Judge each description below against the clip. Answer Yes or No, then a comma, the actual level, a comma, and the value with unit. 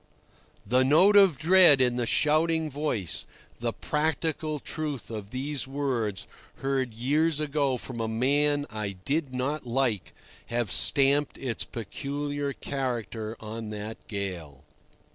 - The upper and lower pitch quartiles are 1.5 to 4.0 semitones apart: No, average, 4.5 semitones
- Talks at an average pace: No, slow, 125 wpm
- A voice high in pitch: No, low, 135 Hz